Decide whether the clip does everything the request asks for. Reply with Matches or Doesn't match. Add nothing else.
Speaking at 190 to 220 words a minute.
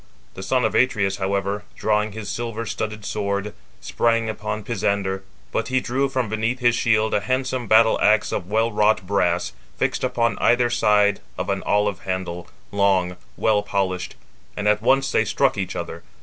Doesn't match